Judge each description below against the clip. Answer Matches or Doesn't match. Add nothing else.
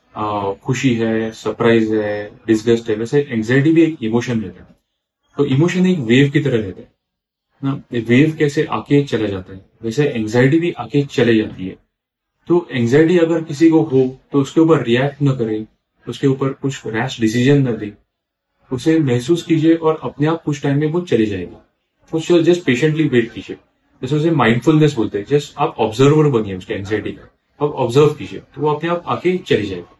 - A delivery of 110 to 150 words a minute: Doesn't match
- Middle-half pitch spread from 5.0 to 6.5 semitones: Matches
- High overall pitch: Doesn't match